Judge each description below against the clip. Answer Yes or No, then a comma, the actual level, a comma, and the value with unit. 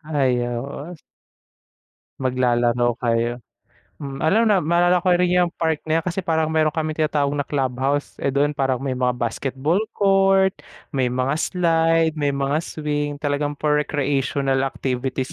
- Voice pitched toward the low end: No, medium, 145 Hz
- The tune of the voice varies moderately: Yes, average, 3.6 semitones